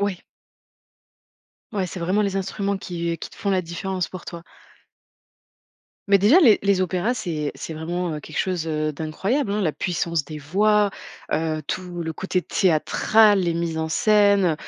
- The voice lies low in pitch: No, medium, 180 Hz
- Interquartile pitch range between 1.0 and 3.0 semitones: No, average, 3.6 semitones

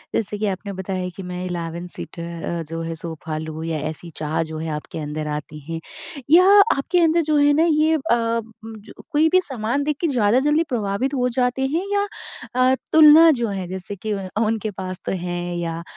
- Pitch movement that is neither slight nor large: No, wide, 8.3 semitones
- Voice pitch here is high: Yes, high, 205 Hz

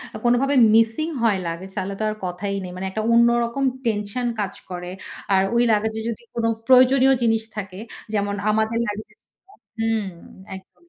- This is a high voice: Yes, high, 220 Hz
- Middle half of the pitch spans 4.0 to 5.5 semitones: No, average, 3.0 semitones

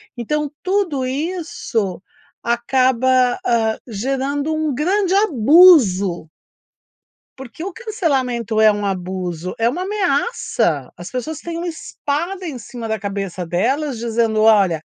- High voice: Yes, very high, 255 Hz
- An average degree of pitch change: No, wide, 6.5 semitones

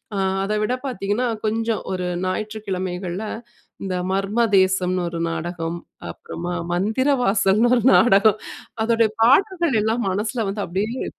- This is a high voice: Yes, high, 205 Hz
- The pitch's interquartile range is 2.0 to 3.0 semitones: No, average, 3.4 semitones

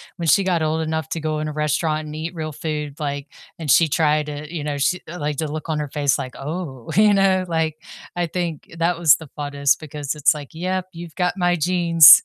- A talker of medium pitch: Yes, medium, 155 Hz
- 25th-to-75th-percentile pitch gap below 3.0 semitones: Yes, narrow, 2.5 semitones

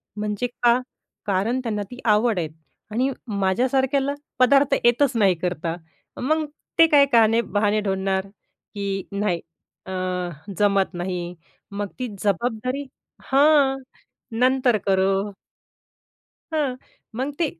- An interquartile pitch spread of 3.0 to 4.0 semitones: No, average, 5.0 semitones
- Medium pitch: No, high, 220 Hz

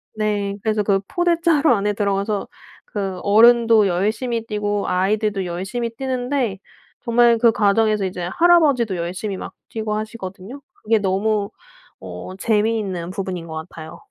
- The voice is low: No, high, 210 Hz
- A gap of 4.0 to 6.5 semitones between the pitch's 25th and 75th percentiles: No, average, 3.1 semitones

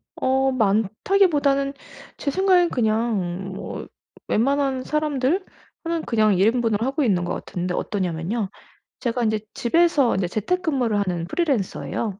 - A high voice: Yes, high, 235 Hz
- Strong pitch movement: Yes, wide, 5.9 semitones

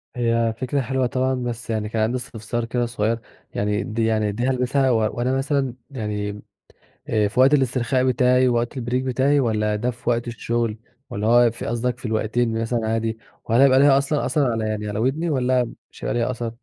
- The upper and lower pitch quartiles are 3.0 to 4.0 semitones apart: No, narrow, 2.4 semitones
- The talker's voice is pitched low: Yes, low, 120 Hz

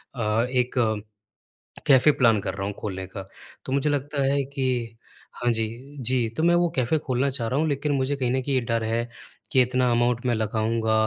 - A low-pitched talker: Yes, low, 125 Hz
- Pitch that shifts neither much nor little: Yes, average, 3.5 semitones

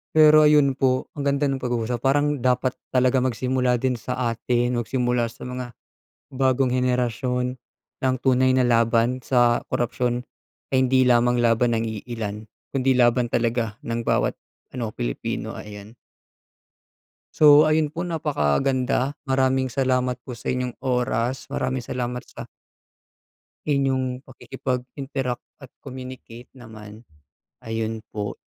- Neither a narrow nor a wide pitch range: No, narrow, 1.8 semitones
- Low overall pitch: Yes, low, 125 Hz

